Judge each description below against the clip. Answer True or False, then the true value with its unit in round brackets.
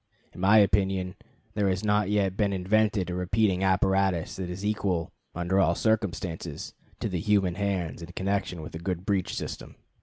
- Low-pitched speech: True (95 Hz)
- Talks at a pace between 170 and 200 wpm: True (175 wpm)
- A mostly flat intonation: True (2.2 semitones)